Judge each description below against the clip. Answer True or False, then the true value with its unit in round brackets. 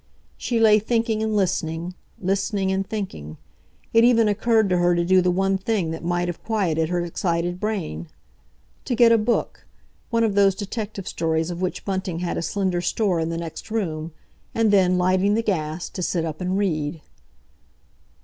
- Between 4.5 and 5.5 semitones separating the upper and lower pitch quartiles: False (3.7 semitones)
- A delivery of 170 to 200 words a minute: True (175 wpm)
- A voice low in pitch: False (185 Hz)